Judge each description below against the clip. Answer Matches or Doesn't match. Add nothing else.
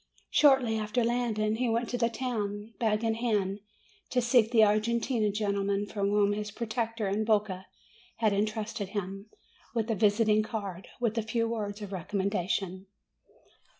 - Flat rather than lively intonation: Matches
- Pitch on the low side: Doesn't match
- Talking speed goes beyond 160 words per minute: Doesn't match